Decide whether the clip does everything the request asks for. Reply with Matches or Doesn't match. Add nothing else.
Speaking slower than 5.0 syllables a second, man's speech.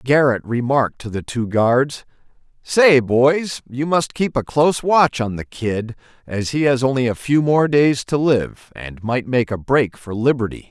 Matches